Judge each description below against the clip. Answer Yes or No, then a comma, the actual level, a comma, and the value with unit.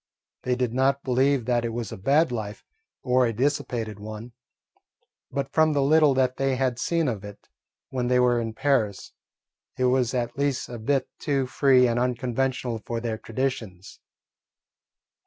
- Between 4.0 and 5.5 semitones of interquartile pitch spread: No, average, 2.7 semitones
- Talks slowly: No, average, 165 wpm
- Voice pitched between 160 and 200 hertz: No, low, 125 Hz